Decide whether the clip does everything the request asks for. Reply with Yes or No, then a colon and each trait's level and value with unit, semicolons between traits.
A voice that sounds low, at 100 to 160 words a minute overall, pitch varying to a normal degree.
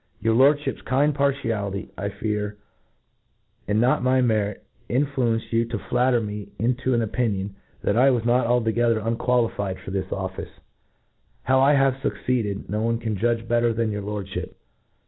Yes: low, 115 Hz; average, 155 wpm; average, 3.2 semitones